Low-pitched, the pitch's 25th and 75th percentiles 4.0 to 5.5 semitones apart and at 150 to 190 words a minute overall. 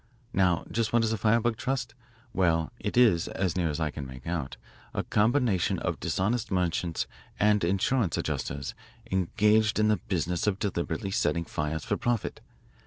Yes: very low, 95 Hz; average, 4.6 semitones; average, 165 wpm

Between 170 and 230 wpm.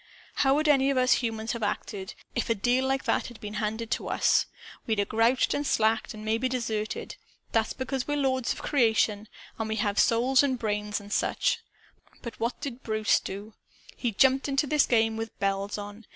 Yes: average, 190 wpm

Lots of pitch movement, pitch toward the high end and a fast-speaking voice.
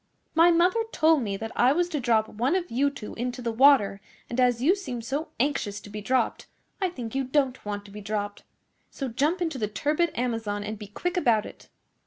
Yes: wide, 5.7 semitones; very high, 250 Hz; fast, 220 wpm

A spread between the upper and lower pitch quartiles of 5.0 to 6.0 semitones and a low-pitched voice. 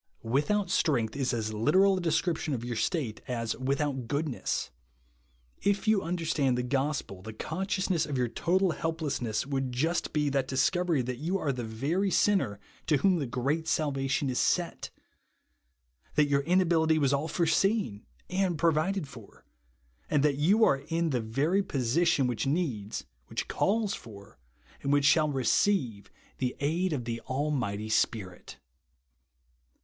No: wide, 5.5 semitones; medium, 145 Hz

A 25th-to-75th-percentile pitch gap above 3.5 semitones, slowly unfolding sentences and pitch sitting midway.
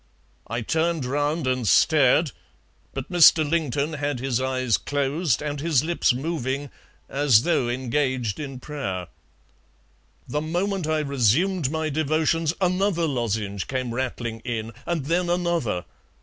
Yes: average, 4.5 semitones; slow, 130 wpm; medium, 145 Hz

